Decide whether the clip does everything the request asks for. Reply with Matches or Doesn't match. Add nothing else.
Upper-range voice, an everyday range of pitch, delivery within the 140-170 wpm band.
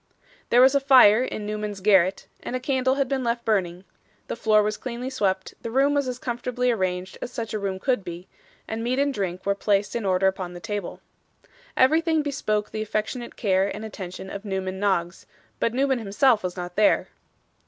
Doesn't match